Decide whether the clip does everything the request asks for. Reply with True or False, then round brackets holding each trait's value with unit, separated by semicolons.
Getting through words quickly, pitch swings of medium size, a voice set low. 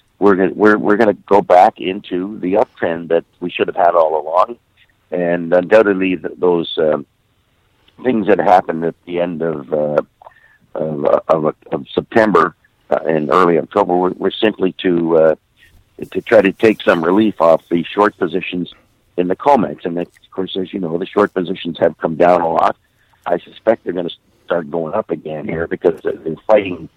False (190 wpm; 3.3 semitones; 90 Hz)